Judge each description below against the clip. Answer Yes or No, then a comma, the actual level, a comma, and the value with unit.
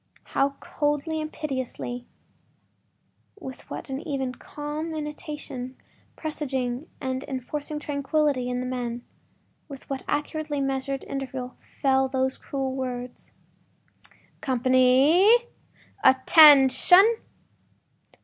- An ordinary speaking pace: No, slow, 85 wpm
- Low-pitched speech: No, very high, 270 Hz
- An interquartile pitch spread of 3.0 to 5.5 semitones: No, narrow, 2.6 semitones